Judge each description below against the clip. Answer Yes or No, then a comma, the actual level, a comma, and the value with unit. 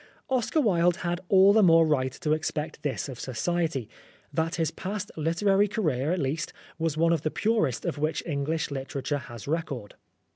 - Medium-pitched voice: Yes, medium, 160 Hz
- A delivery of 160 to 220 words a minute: Yes, average, 175 wpm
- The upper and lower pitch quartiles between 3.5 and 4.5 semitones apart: Yes, average, 3.9 semitones